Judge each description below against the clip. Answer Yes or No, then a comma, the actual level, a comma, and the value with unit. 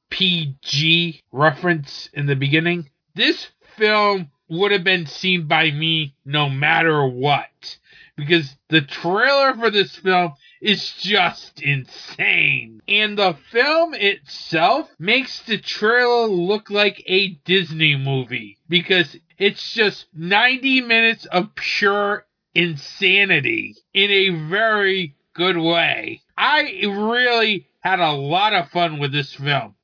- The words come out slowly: Yes, slow, 120 wpm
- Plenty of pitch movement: No, average, 4.6 semitones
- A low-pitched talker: No, medium, 180 Hz